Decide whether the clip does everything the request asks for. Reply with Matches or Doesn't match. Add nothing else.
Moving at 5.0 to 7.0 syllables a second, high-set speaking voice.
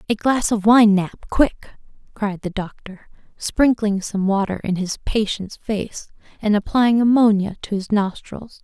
Doesn't match